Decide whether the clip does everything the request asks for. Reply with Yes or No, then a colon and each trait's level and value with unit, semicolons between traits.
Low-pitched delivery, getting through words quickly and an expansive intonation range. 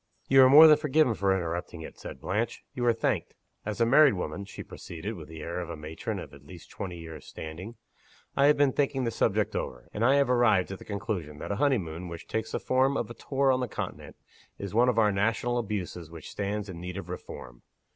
Yes: low, 105 Hz; fast, 235 wpm; wide, 6.6 semitones